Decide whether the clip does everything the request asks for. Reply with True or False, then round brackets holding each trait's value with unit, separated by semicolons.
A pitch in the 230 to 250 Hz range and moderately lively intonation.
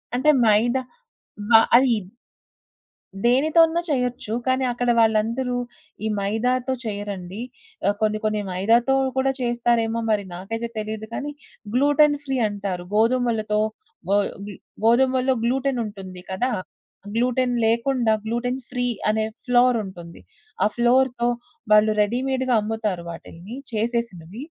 True (235 Hz; 3.0 semitones)